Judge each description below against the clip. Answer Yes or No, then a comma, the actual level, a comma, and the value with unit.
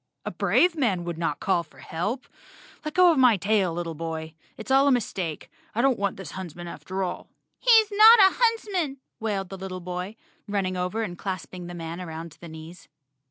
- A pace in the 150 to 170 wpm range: No, average, 190 wpm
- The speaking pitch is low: No, high, 190 Hz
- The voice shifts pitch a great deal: Yes, wide, 7.2 semitones